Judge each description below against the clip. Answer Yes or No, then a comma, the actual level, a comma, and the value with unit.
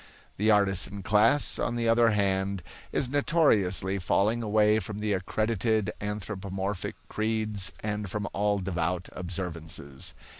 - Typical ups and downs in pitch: No, narrow, 2.2 semitones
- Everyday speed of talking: No, slow, 120 wpm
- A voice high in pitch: No, low, 105 Hz